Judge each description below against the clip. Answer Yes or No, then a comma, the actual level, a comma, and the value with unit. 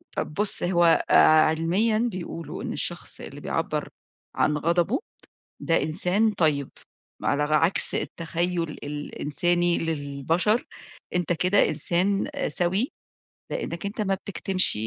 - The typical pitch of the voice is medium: Yes, medium, 175 Hz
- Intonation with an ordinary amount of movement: Yes, average, 3.4 semitones